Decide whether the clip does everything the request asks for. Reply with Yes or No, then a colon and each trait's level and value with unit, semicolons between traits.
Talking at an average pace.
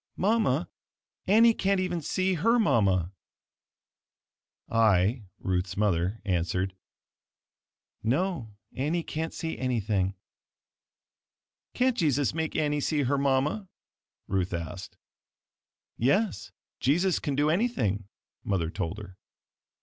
No: slow, 100 wpm